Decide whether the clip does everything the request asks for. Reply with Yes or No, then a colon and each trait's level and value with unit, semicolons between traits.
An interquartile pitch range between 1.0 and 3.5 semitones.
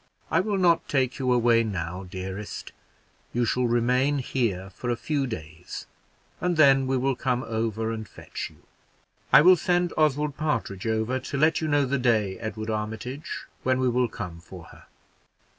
No: average, 4.2 semitones